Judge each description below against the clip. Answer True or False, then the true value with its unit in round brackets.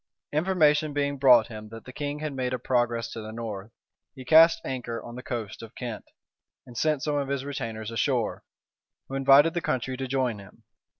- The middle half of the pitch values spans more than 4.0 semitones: False (3.6 semitones)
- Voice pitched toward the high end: False (130 Hz)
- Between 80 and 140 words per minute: False (195 wpm)